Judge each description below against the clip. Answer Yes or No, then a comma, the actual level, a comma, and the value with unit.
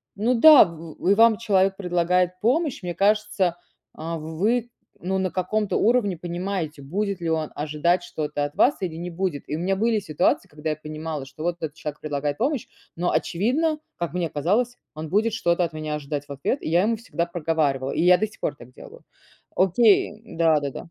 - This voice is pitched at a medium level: Yes, medium, 175 Hz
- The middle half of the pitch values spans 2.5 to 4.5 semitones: No, average, 4.9 semitones